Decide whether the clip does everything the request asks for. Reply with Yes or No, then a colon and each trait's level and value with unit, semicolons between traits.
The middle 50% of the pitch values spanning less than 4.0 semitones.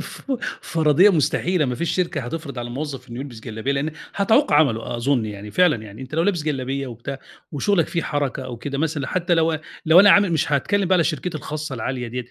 No: average, 4.8 semitones